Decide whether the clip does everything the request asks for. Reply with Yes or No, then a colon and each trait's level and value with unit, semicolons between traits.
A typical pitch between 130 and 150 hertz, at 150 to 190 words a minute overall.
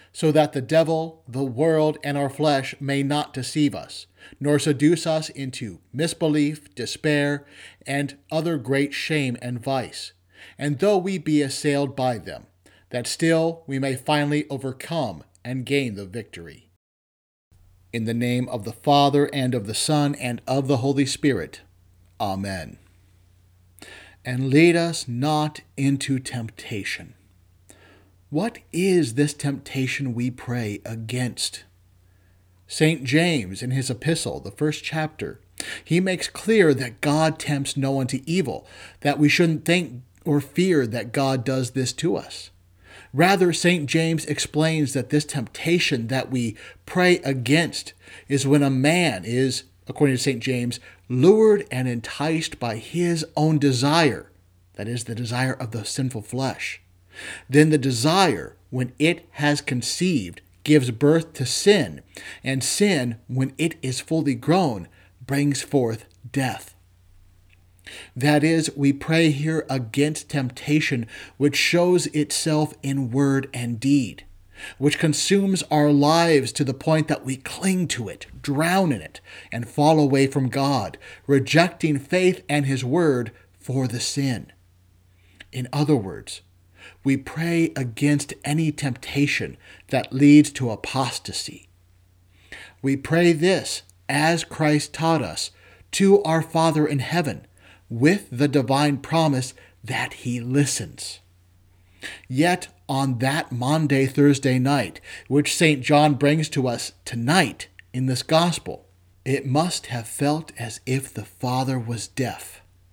No: low, 135 Hz; slow, 135 wpm